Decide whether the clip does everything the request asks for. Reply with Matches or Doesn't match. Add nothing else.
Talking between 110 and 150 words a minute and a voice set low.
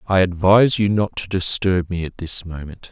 Doesn't match